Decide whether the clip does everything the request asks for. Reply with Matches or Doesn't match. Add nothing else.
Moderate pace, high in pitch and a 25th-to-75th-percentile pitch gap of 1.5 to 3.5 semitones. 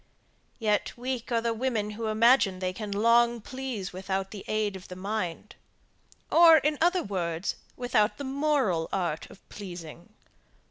Doesn't match